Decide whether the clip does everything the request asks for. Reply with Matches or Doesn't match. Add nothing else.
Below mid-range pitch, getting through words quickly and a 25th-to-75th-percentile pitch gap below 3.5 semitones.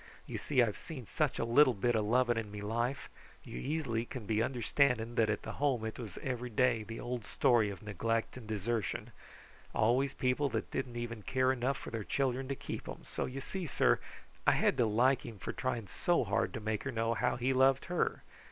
Matches